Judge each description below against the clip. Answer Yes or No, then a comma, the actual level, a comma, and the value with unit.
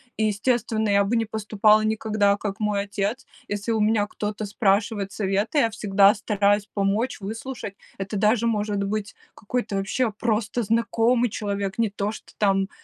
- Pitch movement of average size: No, narrow, 1.8 semitones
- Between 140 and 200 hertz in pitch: No, high, 210 Hz